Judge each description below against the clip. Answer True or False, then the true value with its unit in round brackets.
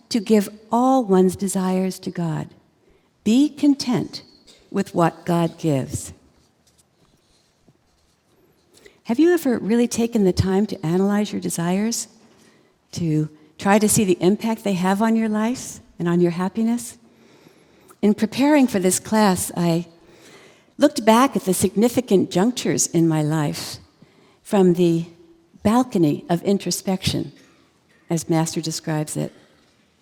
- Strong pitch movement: False (4.7 semitones)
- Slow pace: True (125 wpm)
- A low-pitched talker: False (190 Hz)